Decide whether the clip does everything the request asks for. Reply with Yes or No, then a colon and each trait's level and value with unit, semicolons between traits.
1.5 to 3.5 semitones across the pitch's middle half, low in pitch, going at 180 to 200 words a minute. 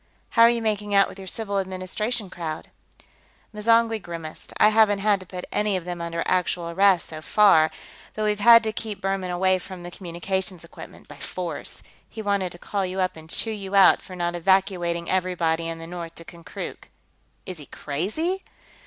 No: average, 3.2 semitones; medium, 185 Hz; average, 190 wpm